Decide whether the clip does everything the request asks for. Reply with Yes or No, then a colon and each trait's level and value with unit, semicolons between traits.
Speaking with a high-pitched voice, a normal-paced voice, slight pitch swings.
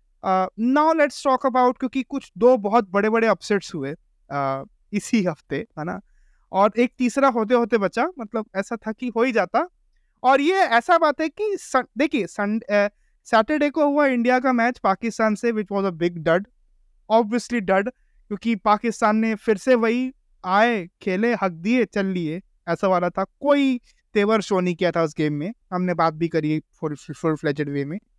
No: high, 220 Hz; average, 170 wpm; average, 5.1 semitones